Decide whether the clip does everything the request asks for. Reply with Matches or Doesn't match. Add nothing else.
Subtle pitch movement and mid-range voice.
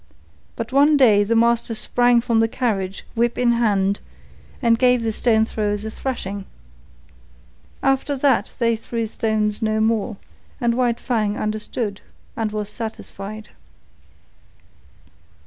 Doesn't match